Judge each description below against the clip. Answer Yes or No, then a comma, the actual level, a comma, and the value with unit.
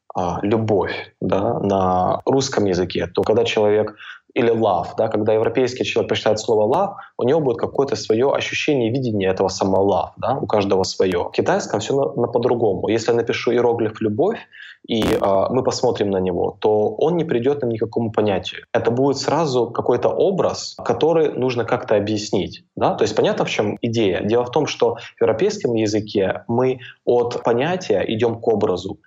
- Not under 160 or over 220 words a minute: Yes, average, 175 wpm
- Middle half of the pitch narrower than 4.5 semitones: Yes, average, 3.4 semitones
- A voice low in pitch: Yes, low, 115 Hz